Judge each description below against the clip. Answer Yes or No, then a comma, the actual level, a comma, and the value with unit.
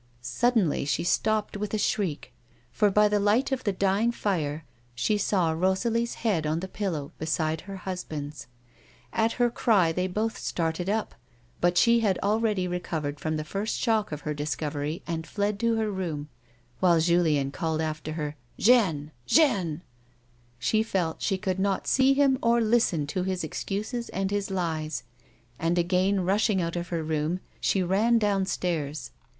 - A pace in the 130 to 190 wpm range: Yes, average, 165 wpm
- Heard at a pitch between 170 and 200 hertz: Yes, medium, 185 Hz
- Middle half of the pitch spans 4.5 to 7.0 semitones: Yes, average, 4.9 semitones